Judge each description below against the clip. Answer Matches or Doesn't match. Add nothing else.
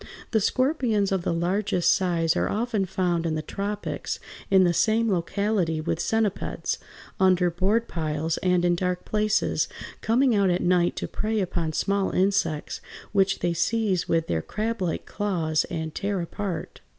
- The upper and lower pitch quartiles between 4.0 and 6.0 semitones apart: Doesn't match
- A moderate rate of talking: Matches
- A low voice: Doesn't match